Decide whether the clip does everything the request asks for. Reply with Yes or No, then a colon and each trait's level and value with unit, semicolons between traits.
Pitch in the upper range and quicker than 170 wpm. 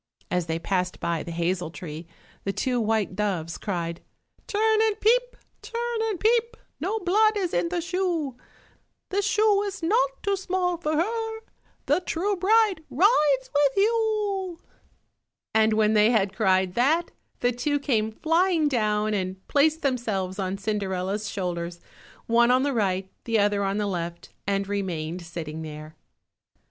No: high, 240 Hz; average, 155 wpm